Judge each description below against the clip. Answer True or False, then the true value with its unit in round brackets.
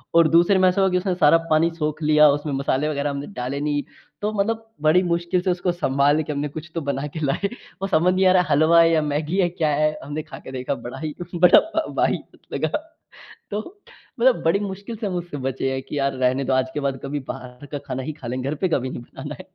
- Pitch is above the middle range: False (155 Hz)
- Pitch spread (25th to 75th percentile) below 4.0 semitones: False (4.3 semitones)